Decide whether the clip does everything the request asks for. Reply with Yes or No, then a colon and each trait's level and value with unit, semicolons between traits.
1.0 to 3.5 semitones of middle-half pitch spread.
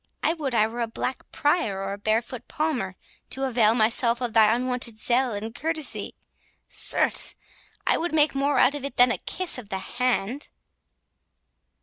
No: average, 3.9 semitones